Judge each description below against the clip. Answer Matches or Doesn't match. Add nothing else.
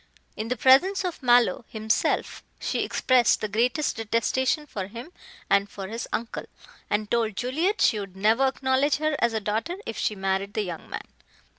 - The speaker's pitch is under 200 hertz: Doesn't match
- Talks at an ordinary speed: Matches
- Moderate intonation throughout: Matches